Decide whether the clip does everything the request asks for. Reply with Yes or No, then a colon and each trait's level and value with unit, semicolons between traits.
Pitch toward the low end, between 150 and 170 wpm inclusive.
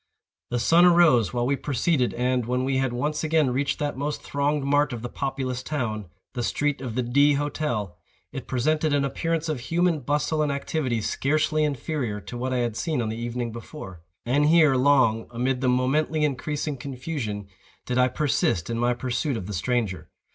No: low, 130 Hz; average, 190 wpm